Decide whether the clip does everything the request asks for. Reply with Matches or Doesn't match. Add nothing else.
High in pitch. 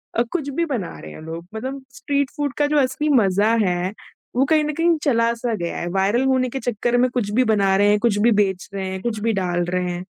Matches